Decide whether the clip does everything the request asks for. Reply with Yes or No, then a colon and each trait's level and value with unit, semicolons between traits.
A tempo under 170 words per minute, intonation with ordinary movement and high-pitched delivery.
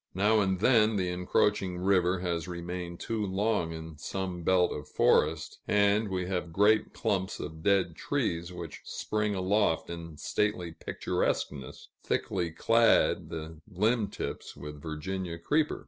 No: average, 145 wpm; average, 3.5 semitones; very low, 90 Hz